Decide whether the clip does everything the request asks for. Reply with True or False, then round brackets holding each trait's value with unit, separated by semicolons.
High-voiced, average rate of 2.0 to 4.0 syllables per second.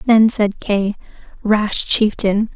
True (210 Hz; 3.1 syllables/s)